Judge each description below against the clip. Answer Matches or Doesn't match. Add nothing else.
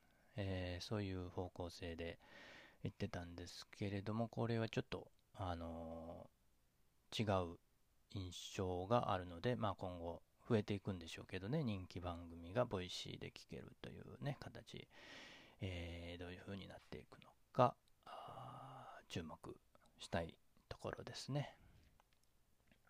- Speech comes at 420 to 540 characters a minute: Doesn't match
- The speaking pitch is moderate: Doesn't match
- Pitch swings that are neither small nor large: Matches